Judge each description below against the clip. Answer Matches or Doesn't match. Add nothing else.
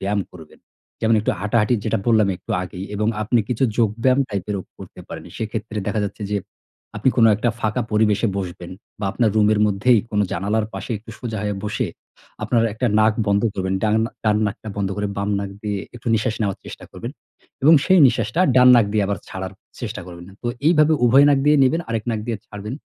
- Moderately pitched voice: Doesn't match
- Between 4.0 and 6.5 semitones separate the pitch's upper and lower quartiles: Doesn't match